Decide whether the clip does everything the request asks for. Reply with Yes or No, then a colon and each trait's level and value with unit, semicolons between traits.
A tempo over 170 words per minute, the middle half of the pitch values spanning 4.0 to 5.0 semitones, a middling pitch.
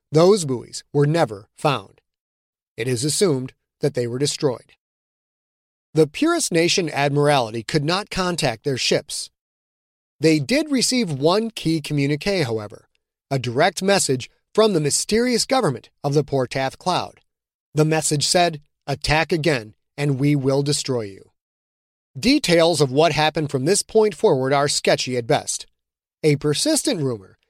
No: average, 140 wpm; average, 4.6 semitones; medium, 150 Hz